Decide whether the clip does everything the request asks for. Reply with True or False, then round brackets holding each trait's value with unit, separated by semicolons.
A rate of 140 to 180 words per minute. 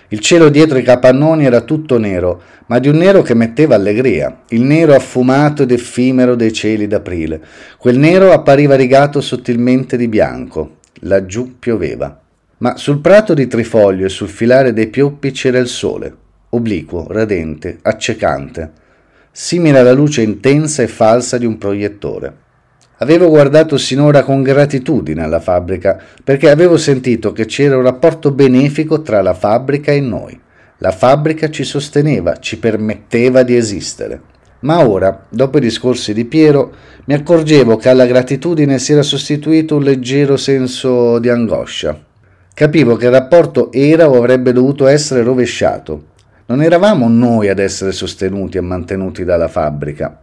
True (150 wpm)